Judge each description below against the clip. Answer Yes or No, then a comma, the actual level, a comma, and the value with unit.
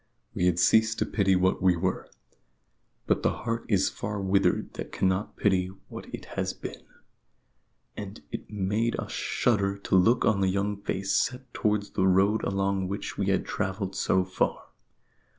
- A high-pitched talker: No, low, 100 Hz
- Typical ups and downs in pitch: No, narrow, 1.9 semitones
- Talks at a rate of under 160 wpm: No, average, 170 wpm